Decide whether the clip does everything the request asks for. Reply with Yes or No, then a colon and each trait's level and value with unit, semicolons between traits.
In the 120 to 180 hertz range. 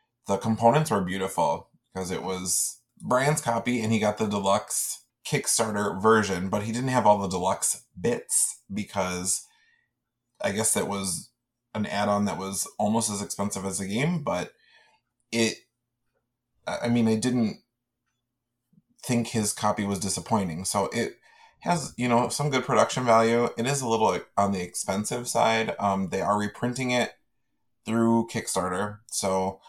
No: low, 110 Hz